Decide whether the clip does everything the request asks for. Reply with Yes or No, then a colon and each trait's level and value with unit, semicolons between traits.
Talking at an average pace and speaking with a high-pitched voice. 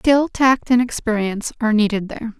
Yes: average, 175 wpm; high, 230 Hz